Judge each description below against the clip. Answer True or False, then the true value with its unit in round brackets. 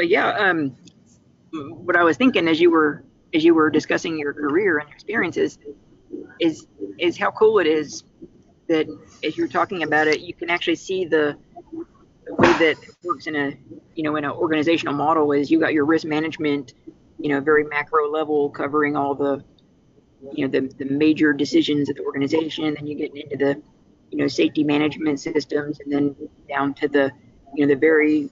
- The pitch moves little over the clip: True (1.9 semitones)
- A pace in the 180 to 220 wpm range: True (190 wpm)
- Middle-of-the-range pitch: True (150 Hz)